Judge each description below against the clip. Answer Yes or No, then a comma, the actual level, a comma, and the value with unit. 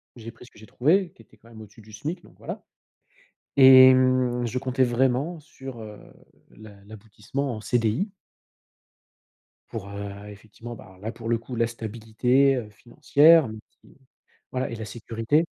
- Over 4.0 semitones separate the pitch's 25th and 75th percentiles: No, average, 3.2 semitones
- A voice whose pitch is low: Yes, low, 120 Hz